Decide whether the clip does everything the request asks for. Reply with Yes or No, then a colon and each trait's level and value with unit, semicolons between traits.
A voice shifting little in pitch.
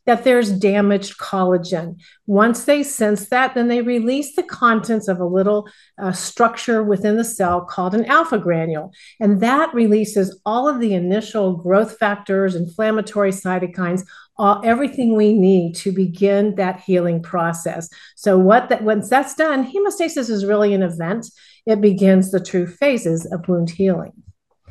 No: average, 3.8 semitones